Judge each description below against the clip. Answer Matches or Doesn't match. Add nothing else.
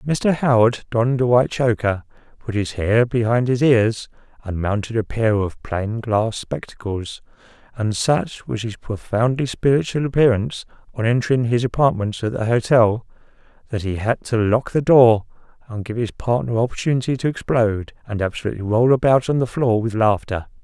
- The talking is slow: Doesn't match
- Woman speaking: Doesn't match